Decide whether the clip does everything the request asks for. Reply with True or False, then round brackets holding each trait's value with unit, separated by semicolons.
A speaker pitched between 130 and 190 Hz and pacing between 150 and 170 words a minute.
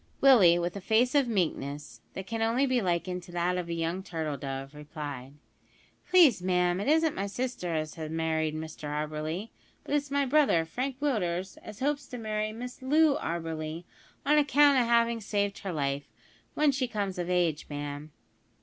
False (185 Hz; 180 wpm)